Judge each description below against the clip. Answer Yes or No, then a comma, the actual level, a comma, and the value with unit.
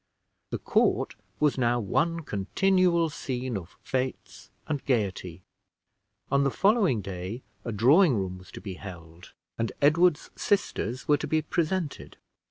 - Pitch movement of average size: No, wide, 8.3 semitones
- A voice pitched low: Yes, low, 130 Hz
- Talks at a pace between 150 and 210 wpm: No, average, 140 wpm